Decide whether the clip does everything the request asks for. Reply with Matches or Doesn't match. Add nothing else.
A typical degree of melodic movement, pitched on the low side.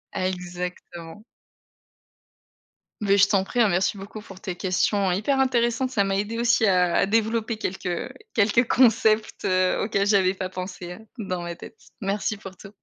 Doesn't match